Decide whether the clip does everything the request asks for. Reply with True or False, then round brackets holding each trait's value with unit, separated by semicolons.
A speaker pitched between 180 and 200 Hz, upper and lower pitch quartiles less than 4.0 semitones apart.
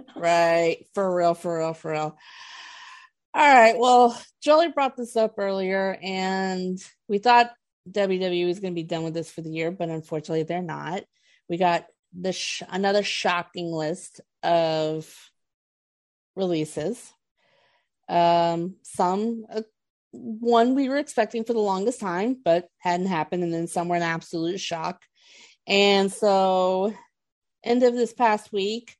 False (190 Hz; 4.9 semitones)